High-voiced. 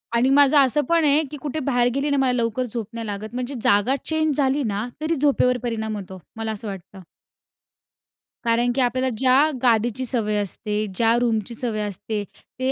Yes: high, 245 Hz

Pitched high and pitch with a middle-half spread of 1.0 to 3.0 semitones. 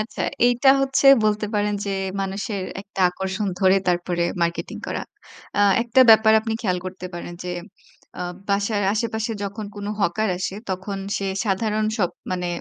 Yes: high, 200 Hz; narrow, 2.6 semitones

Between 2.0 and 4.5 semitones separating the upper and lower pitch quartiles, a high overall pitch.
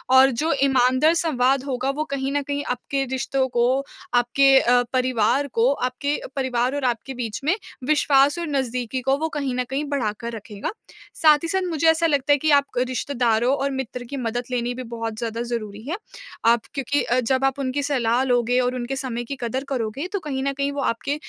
Yes: average, 2.7 semitones; very high, 260 Hz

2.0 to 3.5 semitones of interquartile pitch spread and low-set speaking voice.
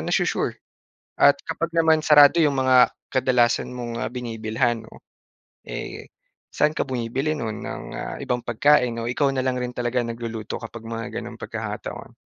Yes: average, 2.8 semitones; low, 125 Hz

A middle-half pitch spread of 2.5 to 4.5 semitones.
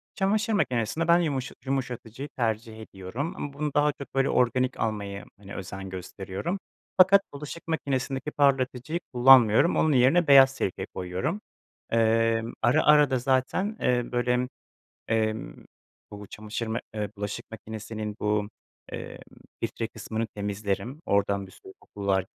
No: average, 5.0 semitones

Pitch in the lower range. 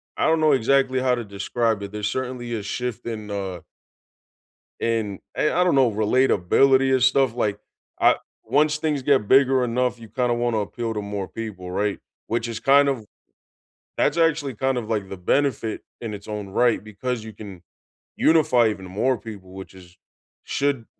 Yes: low, 120 Hz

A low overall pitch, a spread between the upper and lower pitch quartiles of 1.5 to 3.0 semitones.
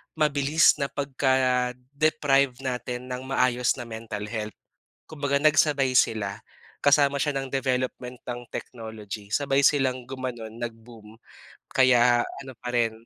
Yes: low, 130 Hz; narrow, 2.5 semitones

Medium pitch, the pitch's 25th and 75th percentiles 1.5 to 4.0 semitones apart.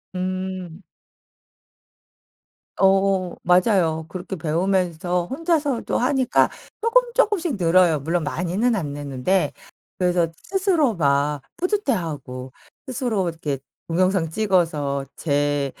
No: medium, 180 Hz; wide, 6.0 semitones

